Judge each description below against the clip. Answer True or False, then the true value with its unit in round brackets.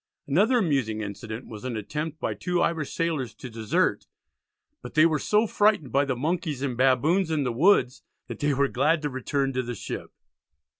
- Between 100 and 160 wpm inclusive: False (190 wpm)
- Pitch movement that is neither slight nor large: True (4.7 semitones)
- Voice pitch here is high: False (140 Hz)